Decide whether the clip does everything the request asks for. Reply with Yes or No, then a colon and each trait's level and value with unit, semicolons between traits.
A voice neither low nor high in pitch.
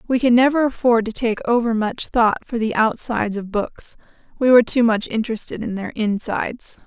No: high, 230 Hz